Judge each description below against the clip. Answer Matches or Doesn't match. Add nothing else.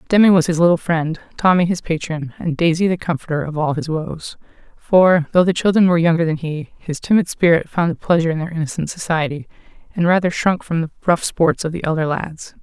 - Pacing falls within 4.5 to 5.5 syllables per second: Doesn't match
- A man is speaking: Doesn't match